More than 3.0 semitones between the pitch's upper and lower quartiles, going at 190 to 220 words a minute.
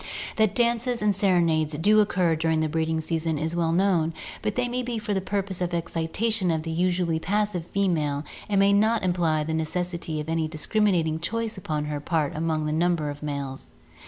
Yes: average, 4.1 semitones; average, 195 wpm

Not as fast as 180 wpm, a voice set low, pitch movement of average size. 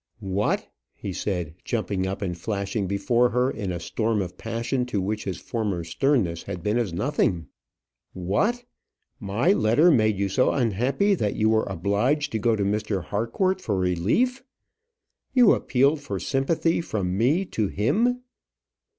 No: average, 155 wpm; low, 110 Hz; wide, 5.7 semitones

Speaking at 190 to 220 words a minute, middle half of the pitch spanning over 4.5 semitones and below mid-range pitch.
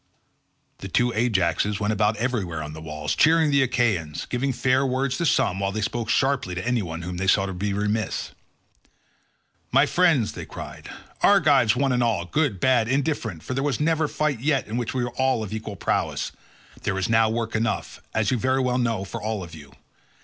Yes: average, 200 wpm; average, 5.1 semitones; low, 115 Hz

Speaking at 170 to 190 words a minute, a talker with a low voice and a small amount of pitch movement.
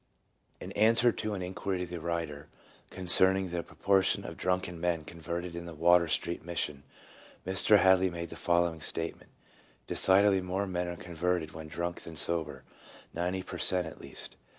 Yes: average, 175 wpm; very low, 85 Hz; narrow, 1.9 semitones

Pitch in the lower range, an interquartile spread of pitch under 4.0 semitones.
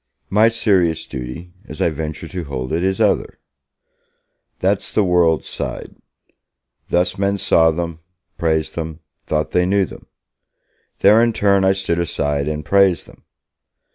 Yes: very low, 85 Hz; average, 3.5 semitones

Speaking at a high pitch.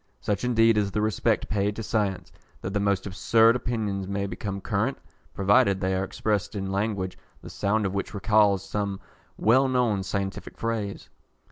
No: low, 100 Hz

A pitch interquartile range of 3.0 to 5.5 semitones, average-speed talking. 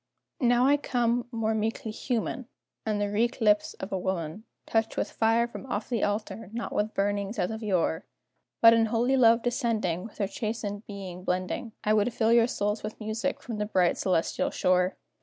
No: narrow, 2.5 semitones; average, 190 wpm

